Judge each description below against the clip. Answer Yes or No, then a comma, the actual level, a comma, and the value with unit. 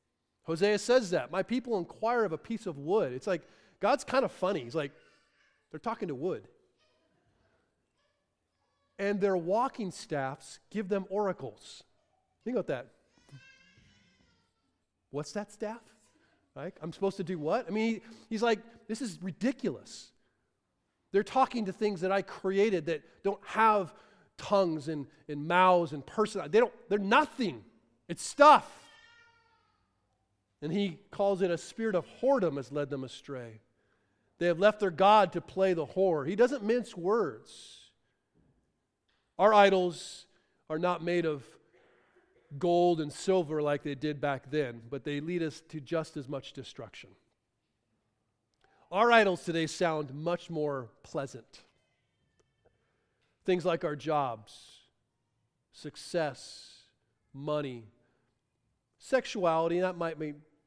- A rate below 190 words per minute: Yes, slow, 135 wpm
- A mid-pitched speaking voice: Yes, medium, 170 Hz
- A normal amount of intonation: No, wide, 6.4 semitones